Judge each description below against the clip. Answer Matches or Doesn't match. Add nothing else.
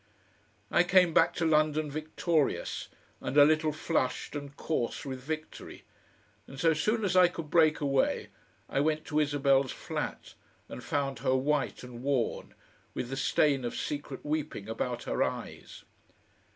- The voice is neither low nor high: Matches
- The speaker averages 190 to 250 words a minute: Doesn't match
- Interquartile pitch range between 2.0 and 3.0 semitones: Matches